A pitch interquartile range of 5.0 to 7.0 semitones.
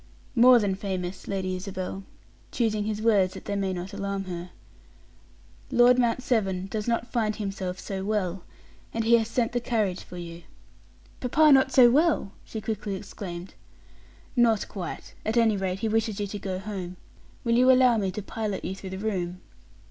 No: average, 3.5 semitones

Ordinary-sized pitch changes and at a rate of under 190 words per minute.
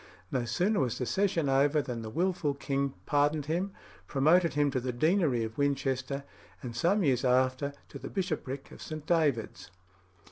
Yes: average, 3.7 semitones; average, 170 wpm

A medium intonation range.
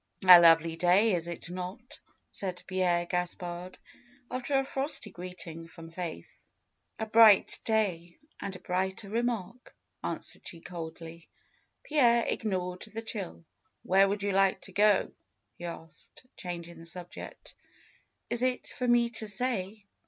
Yes: average, 4.2 semitones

